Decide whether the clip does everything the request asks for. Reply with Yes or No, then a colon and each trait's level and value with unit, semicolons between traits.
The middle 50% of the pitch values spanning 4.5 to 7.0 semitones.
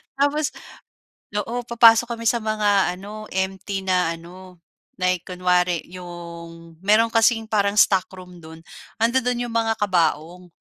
No: average, 4.1 semitones